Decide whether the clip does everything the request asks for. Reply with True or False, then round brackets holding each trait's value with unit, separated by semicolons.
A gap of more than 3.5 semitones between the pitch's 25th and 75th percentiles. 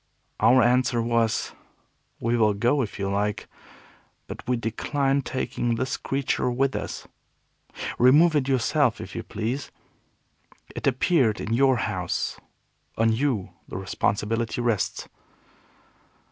False (3.2 semitones)